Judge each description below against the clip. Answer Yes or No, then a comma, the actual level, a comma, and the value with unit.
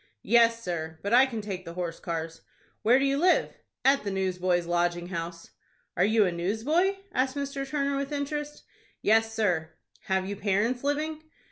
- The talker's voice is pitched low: No, high, 215 Hz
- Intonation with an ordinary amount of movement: No, wide, 7.5 semitones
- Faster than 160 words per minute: Yes, average, 170 wpm